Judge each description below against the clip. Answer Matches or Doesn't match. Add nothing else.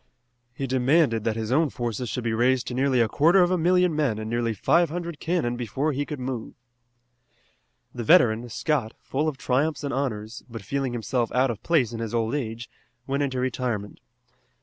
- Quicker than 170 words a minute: Matches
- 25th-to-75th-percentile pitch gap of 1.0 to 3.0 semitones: Doesn't match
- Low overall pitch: Matches